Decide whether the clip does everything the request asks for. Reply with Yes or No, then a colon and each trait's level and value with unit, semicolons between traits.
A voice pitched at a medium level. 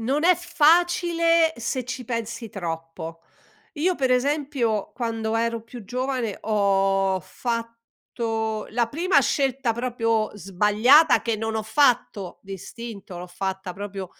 No: high, 230 Hz